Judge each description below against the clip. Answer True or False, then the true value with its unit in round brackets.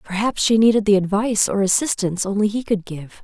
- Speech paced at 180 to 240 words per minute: True (205 wpm)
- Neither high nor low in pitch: False (205 Hz)